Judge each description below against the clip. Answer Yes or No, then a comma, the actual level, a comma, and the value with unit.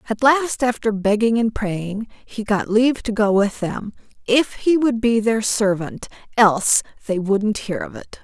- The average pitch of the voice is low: No, high, 220 Hz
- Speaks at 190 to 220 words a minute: No, average, 180 wpm